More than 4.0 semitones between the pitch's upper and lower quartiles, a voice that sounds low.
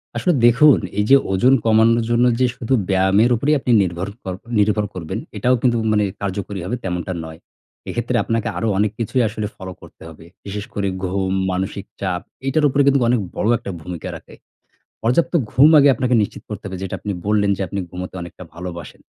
Yes: average, 4.4 semitones; low, 105 Hz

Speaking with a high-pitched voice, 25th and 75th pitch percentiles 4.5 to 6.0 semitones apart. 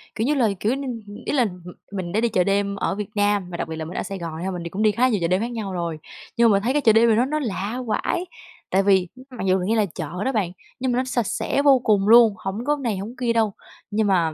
No: high, 210 Hz; average, 4.0 semitones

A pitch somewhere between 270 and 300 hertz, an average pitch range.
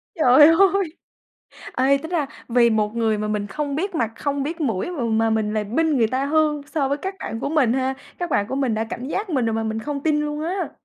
No: very high, 275 Hz; wide, 5.7 semitones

